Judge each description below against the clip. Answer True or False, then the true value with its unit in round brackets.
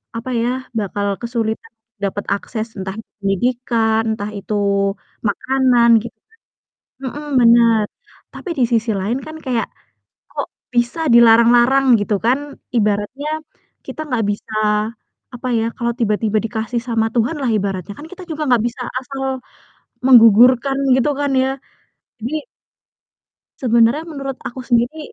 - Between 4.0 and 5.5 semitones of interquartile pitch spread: False (3.1 semitones)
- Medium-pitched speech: False (235 Hz)